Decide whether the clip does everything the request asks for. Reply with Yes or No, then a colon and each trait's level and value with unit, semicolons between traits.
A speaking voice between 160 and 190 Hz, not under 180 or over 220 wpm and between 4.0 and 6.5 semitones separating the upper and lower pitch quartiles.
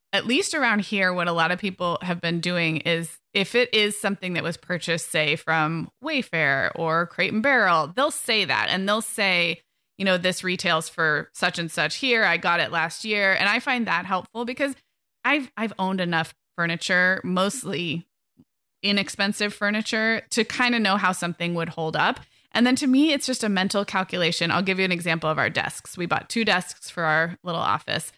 Yes: medium, 185 Hz; average, 200 wpm; average, 4.3 semitones